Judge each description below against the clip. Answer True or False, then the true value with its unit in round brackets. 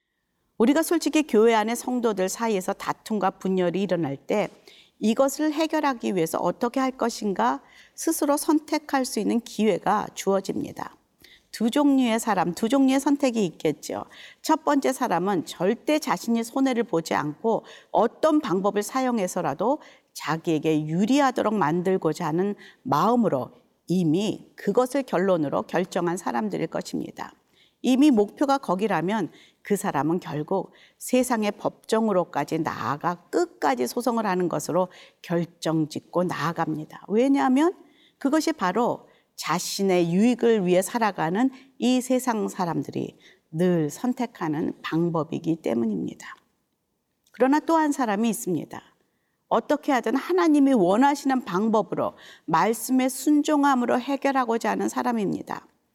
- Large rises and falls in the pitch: True (7.1 semitones)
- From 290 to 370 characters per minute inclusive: True (305 characters per minute)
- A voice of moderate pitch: False (225 Hz)